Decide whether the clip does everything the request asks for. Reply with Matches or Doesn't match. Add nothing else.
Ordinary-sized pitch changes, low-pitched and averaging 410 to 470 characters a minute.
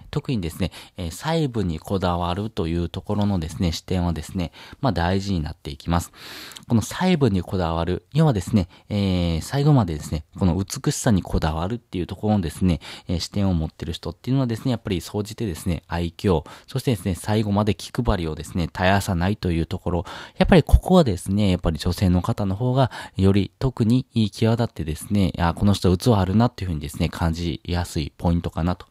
Matches